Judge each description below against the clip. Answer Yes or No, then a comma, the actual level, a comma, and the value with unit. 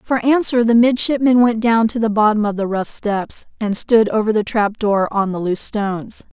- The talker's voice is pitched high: Yes, high, 220 Hz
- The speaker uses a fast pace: Yes, fast, 215 wpm